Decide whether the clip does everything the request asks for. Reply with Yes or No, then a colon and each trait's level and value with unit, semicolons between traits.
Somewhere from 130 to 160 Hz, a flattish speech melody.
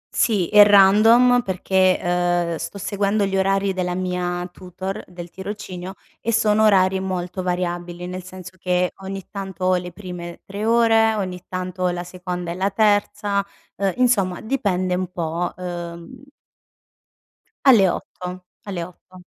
No: medium, 185 Hz; narrow, 2.0 semitones